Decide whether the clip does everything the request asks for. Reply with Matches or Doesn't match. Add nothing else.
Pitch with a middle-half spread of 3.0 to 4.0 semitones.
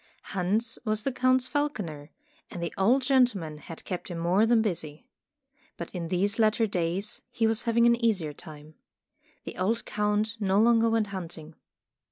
Doesn't match